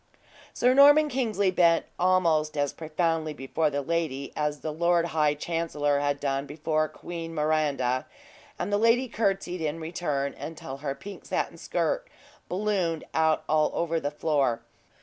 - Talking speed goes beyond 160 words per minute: No, average, 150 wpm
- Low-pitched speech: No, medium, 160 Hz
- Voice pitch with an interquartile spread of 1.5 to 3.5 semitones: Yes, average, 3.2 semitones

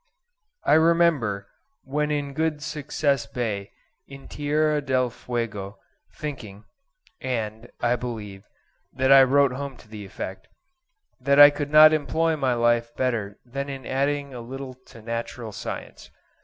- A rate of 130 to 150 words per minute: Yes, average, 140 wpm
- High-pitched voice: No, low, 130 Hz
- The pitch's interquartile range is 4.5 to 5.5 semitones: No, average, 3.9 semitones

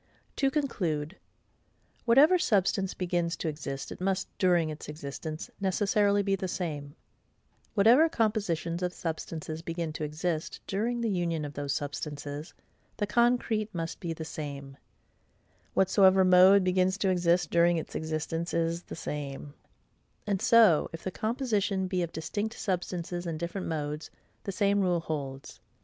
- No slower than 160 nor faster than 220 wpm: No, average, 145 wpm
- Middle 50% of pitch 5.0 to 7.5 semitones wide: No, average, 4.1 semitones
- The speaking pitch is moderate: Yes, medium, 175 Hz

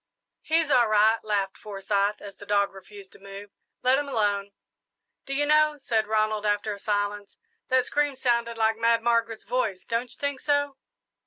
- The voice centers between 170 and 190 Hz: No, high, 220 Hz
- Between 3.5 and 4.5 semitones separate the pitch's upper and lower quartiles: Yes, average, 3.9 semitones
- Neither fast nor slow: Yes, average, 175 wpm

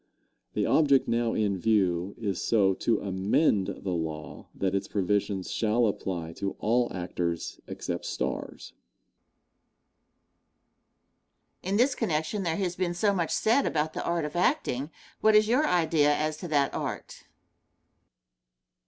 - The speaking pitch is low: Yes, low, 120 Hz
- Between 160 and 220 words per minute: No, average, 140 wpm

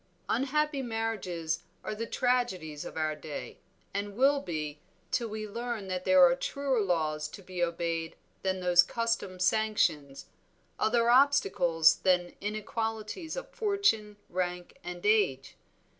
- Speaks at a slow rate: Yes, slow, 130 wpm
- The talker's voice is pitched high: Yes, high, 195 Hz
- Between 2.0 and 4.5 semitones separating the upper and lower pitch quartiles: No, average, 4.9 semitones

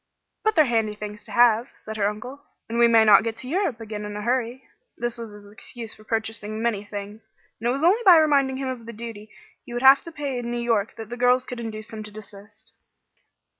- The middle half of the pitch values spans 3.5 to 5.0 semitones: No, average, 2.8 semitones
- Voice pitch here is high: Yes, high, 230 Hz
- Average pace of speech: No, fast, 240 wpm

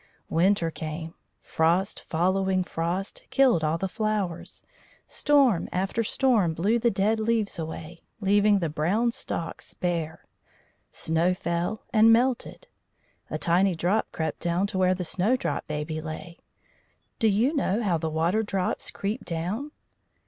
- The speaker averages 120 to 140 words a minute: Yes, slow, 135 wpm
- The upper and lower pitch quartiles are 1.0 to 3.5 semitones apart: No, average, 4.4 semitones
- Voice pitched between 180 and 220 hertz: Yes, medium, 185 Hz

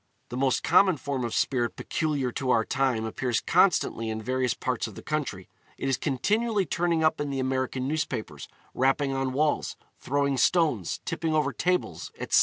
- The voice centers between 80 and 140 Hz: Yes, low, 135 Hz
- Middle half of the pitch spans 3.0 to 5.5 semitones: Yes, average, 3.8 semitones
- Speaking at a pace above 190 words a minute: No, average, 175 wpm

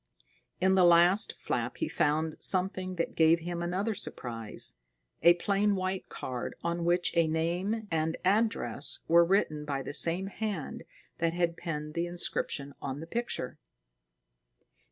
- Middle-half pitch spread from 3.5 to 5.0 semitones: No, average, 3.0 semitones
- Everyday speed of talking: Yes, average, 145 wpm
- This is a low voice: No, medium, 170 Hz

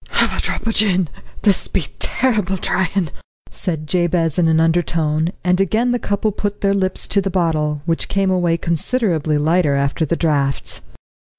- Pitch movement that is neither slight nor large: Yes, average, 3.6 semitones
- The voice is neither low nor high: Yes, medium, 175 Hz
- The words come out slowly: No, average, 170 wpm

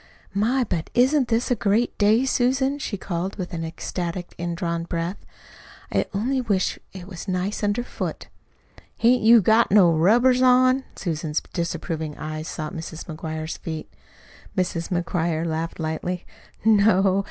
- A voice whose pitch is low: No, medium, 185 Hz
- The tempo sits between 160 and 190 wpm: No, average, 145 wpm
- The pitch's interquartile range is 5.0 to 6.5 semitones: Yes, wide, 5.6 semitones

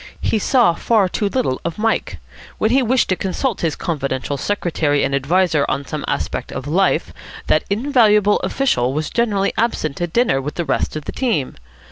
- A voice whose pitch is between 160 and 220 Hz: Yes, medium, 185 Hz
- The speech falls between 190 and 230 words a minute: No, average, 180 wpm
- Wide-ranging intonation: Yes, wide, 7.3 semitones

